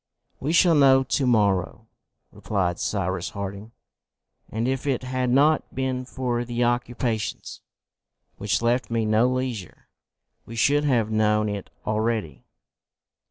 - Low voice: Yes, low, 120 Hz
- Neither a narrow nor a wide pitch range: Yes, average, 3.3 semitones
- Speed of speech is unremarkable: No, slow, 125 wpm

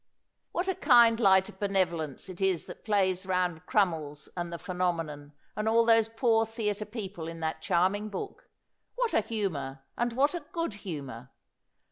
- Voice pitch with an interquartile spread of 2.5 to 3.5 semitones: No, average, 5.0 semitones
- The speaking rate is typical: Yes, average, 165 wpm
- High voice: Yes, high, 195 Hz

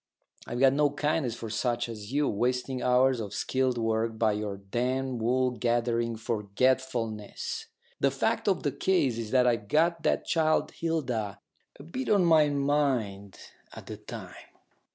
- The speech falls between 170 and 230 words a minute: No, average, 155 wpm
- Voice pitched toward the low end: Yes, low, 125 Hz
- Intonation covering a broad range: No, average, 3.6 semitones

